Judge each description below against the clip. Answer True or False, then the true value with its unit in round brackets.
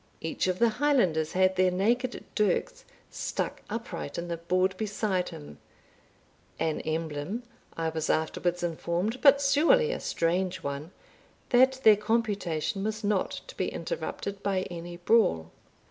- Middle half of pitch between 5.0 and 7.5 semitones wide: True (5.3 semitones)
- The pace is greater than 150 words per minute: False (140 wpm)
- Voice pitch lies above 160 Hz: True (190 Hz)